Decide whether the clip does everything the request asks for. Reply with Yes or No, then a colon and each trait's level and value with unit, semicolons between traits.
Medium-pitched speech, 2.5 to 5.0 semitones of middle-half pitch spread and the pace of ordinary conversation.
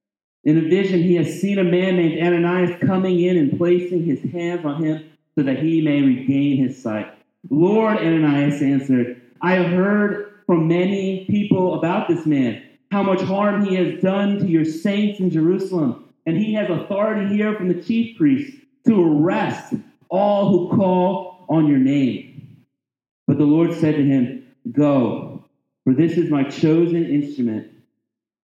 Yes: medium, 175 Hz; average, 4.6 semitones; average, 165 wpm